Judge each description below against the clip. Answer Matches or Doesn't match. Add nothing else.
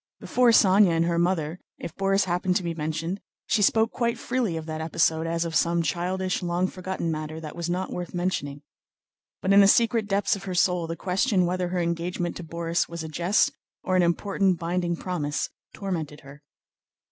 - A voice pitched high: Doesn't match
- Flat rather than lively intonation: Matches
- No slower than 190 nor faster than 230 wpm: Matches